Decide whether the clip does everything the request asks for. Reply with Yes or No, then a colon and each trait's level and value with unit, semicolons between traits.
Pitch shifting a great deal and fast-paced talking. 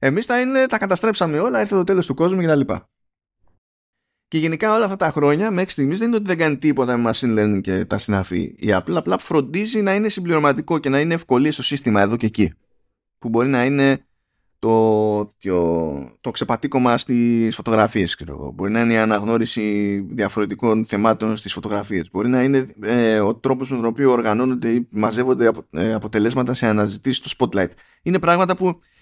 Yes: wide, 6.0 semitones; fast, 190 wpm